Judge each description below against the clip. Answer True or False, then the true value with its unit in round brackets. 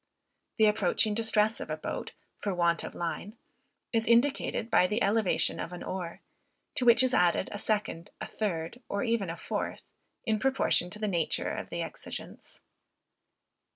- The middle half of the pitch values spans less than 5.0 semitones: True (4.2 semitones)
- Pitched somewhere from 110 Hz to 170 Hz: False (210 Hz)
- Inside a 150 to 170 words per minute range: True (165 wpm)